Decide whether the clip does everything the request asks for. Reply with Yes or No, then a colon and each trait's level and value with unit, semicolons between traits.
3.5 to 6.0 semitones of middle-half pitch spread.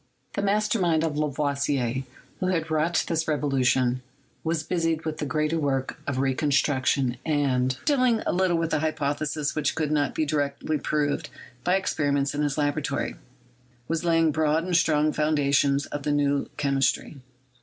No: narrow, 2.4 semitones